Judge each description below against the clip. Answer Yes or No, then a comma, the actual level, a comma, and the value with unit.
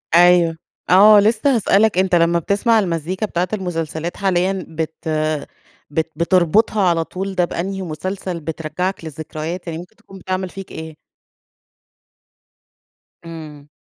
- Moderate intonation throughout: Yes, average, 3.0 semitones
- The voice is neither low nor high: Yes, medium, 180 Hz